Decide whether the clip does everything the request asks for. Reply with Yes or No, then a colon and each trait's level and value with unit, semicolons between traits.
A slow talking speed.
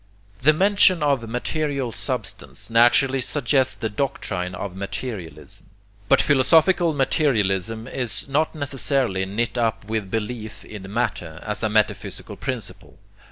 Yes: slow, 120 wpm